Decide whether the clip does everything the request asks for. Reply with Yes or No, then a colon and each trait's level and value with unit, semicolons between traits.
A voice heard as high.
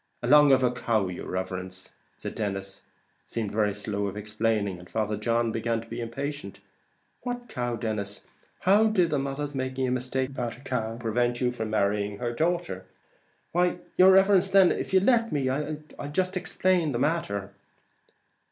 No: low, 120 Hz